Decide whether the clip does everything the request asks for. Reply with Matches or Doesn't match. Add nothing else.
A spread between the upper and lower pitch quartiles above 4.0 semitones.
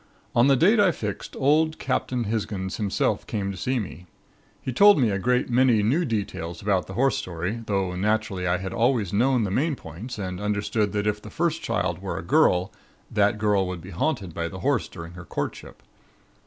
Matches